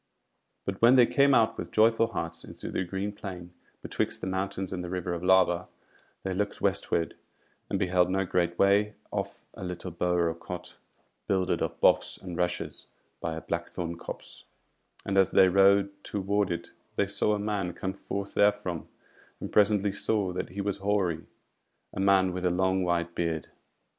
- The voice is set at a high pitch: No, very low, 95 Hz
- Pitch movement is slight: Yes, narrow, 2.2 semitones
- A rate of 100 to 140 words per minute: No, average, 175 wpm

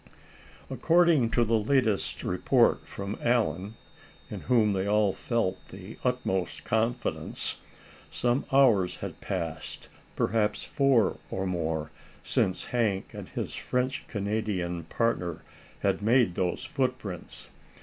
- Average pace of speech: No, slow, 115 wpm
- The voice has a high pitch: No, low, 110 Hz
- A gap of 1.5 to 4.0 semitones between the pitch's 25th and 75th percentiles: No, average, 4.5 semitones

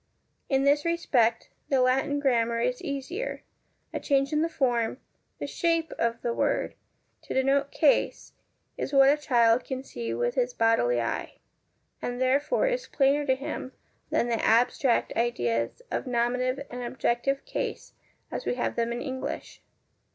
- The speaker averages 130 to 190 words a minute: Yes, average, 155 wpm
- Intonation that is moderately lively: Yes, average, 3.1 semitones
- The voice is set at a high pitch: Yes, very high, 255 Hz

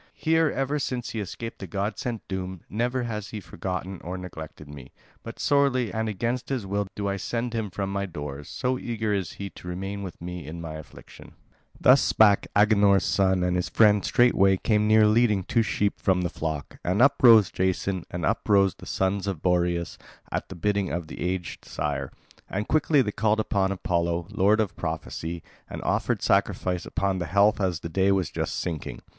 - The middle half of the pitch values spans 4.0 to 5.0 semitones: No, average, 3.5 semitones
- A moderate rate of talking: Yes, average, 195 wpm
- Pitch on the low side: Yes, low, 100 Hz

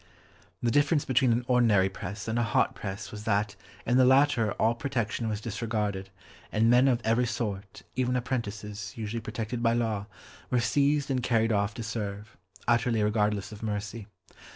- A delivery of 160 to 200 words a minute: Yes, average, 170 wpm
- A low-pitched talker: Yes, low, 115 Hz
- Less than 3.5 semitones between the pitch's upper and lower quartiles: Yes, average, 2.7 semitones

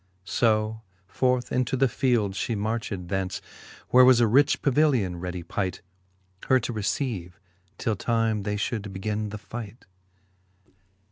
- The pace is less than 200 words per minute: Yes, slow, 135 wpm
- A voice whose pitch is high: No, low, 110 Hz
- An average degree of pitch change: Yes, average, 3.8 semitones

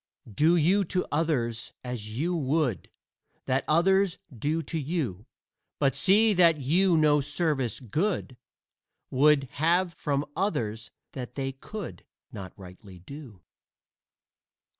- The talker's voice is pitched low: No, medium, 145 Hz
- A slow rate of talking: Yes, slow, 120 wpm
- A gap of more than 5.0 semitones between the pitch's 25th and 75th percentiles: Yes, wide, 5.6 semitones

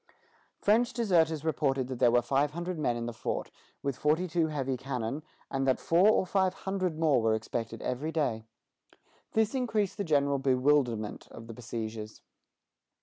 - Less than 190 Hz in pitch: Yes, medium, 140 Hz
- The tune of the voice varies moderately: No, wide, 6.1 semitones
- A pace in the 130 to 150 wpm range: No, average, 165 wpm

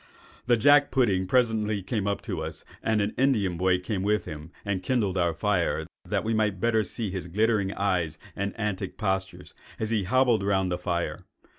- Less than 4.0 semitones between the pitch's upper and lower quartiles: Yes, average, 3.1 semitones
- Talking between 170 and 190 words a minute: Yes, average, 180 wpm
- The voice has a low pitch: Yes, low, 100 Hz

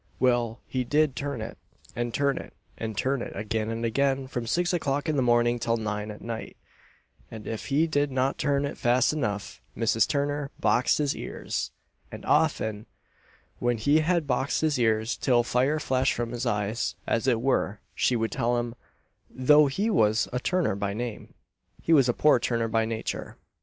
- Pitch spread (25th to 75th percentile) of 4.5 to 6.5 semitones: No, average, 3.8 semitones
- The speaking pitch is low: Yes, low, 120 Hz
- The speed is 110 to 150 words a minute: No, average, 185 wpm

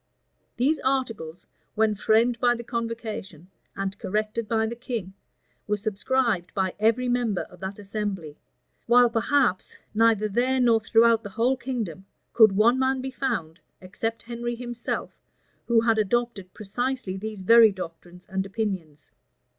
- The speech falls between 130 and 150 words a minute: Yes, average, 140 wpm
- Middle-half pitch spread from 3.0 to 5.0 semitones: Yes, average, 3.7 semitones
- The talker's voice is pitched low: No, high, 225 Hz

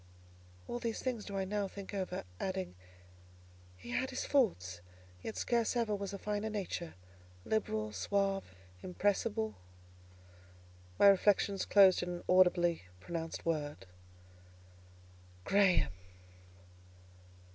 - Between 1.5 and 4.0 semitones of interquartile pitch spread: Yes, average, 3.3 semitones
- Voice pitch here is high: Yes, high, 195 Hz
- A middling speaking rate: No, slow, 110 wpm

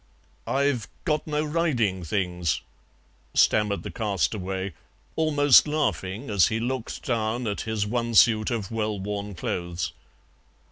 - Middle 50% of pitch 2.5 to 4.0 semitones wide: No, average, 4.8 semitones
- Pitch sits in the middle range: No, low, 110 Hz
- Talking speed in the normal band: No, slow, 125 wpm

